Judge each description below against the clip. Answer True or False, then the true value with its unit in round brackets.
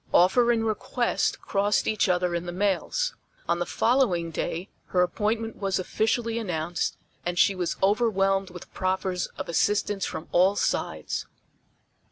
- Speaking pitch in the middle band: False (195 Hz)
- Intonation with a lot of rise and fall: False (3.5 semitones)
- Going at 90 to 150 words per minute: True (145 wpm)